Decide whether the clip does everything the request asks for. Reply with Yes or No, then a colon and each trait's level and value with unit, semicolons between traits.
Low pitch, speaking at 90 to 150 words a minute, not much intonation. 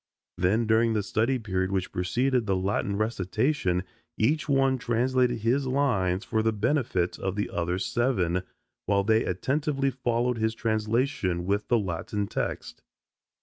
No: low, 110 Hz; average, 145 wpm; average, 4.7 semitones